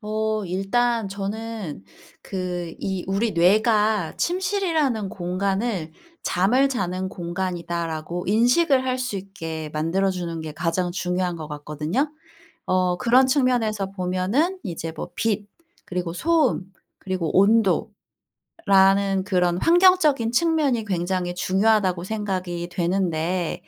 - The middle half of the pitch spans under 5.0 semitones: Yes, average, 4.5 semitones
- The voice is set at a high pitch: Yes, high, 195 Hz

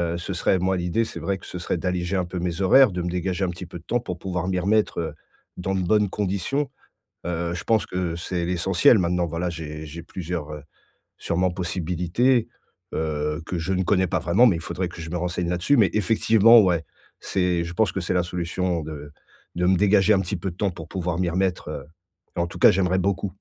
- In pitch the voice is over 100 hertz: No, very low, 90 Hz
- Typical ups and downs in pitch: No, narrow, 2.0 semitones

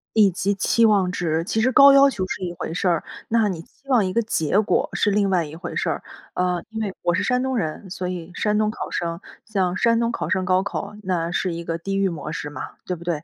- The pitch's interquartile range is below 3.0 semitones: No, average, 3.7 semitones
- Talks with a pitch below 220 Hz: Yes, high, 190 Hz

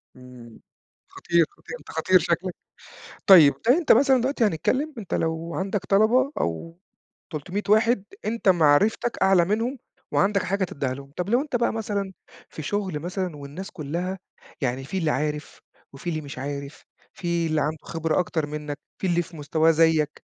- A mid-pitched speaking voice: Yes, medium, 170 Hz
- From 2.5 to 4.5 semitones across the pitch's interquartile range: No, average, 4.9 semitones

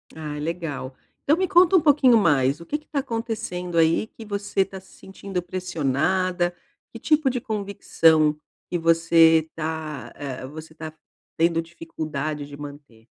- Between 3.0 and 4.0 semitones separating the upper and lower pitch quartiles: No, average, 4.8 semitones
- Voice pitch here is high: No, medium, 165 Hz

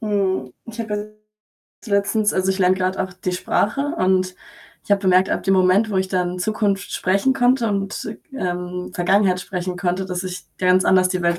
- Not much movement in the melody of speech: Yes, narrow, 2.0 semitones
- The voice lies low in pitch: No, high, 190 Hz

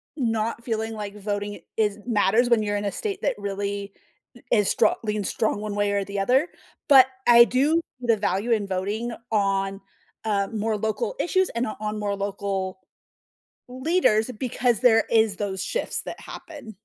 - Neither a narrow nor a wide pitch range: Yes, average, 3.0 semitones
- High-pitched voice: Yes, high, 215 Hz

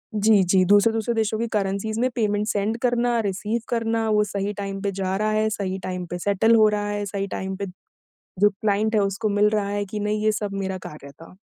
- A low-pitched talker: No, high, 205 Hz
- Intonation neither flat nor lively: No, narrow, 1.7 semitones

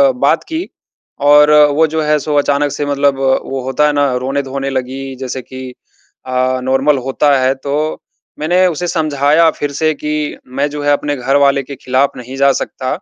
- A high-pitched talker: No, medium, 140 Hz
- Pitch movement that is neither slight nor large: No, narrow, 2.1 semitones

